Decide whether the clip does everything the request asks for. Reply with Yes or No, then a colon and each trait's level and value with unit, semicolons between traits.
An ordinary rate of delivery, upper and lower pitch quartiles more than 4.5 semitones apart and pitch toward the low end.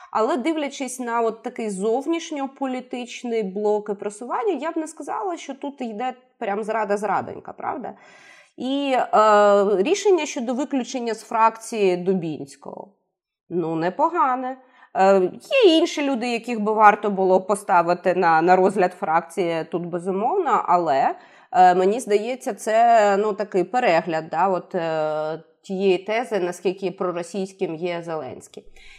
No: average, 125 wpm; wide, 5.6 semitones; high, 215 Hz